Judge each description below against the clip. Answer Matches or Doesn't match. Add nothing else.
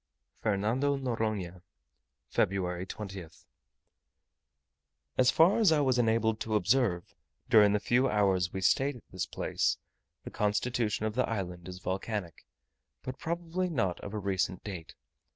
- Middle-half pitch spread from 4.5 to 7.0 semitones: Matches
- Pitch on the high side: Doesn't match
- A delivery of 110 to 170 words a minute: Matches